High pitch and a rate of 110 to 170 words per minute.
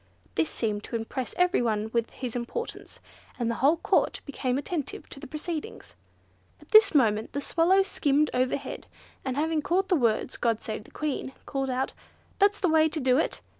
No: very high, 275 Hz; average, 185 wpm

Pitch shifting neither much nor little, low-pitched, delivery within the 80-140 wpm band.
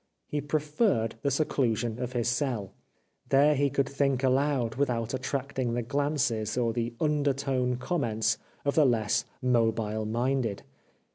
Yes: average, 3.4 semitones; low, 125 Hz; slow, 135 wpm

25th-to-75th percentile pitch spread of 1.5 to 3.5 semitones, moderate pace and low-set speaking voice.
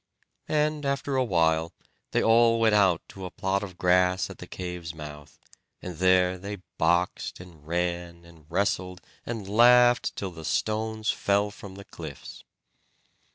No: average, 3.9 semitones; average, 155 wpm; very low, 95 Hz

